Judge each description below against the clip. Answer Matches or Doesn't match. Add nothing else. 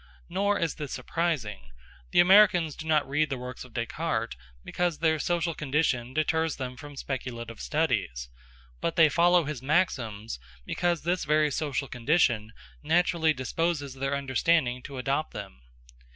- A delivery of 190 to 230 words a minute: Doesn't match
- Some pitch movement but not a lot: Matches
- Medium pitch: Matches